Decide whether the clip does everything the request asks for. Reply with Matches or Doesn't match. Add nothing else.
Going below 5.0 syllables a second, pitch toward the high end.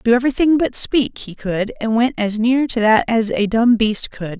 Matches